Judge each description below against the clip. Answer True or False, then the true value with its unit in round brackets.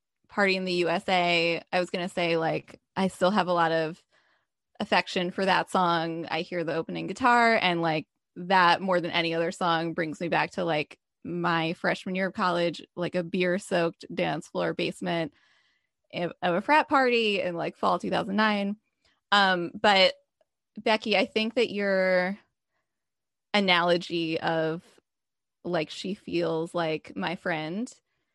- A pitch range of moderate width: True (3.1 semitones)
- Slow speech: False (155 wpm)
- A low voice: False (180 Hz)